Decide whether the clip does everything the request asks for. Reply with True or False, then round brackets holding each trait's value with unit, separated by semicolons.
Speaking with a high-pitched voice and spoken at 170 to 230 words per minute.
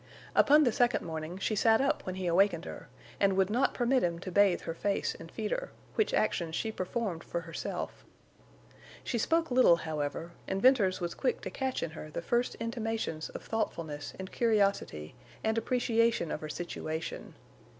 True (195 Hz; 180 wpm)